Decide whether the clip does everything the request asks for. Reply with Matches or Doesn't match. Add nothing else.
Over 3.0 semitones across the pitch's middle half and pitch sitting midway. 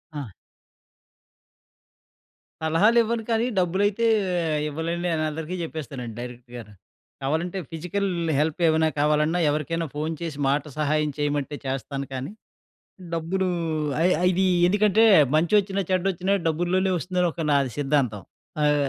Matches